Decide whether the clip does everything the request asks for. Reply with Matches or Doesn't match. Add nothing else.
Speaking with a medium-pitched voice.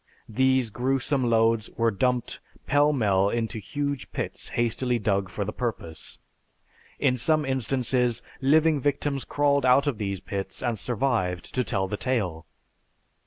Doesn't match